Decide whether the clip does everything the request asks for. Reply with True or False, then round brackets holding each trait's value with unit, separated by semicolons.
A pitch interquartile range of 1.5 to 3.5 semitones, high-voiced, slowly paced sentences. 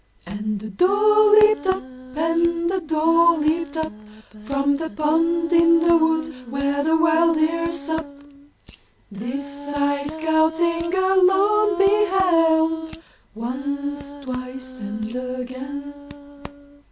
True (3.2 semitones; 320 Hz; 105 wpm)